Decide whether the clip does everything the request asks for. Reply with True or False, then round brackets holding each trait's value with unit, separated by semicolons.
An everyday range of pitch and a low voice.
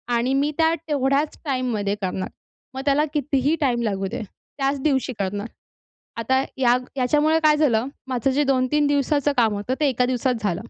False (3.4 semitones; 265 Hz)